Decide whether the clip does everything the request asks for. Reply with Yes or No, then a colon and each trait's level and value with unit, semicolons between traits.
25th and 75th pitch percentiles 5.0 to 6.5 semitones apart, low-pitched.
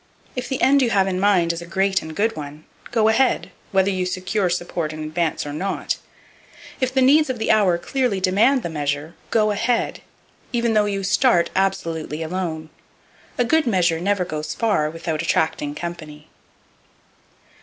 No: wide, 5.4 semitones; medium, 185 Hz